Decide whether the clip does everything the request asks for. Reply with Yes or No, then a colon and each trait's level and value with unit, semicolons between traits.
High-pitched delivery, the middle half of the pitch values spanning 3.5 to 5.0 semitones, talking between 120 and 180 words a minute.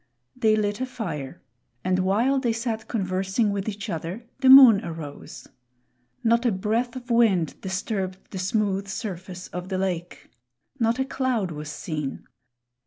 Yes: high, 200 Hz; average, 4.0 semitones; average, 150 wpm